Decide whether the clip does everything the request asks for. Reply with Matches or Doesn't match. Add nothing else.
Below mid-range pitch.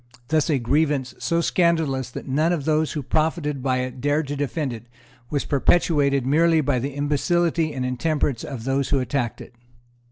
Doesn't match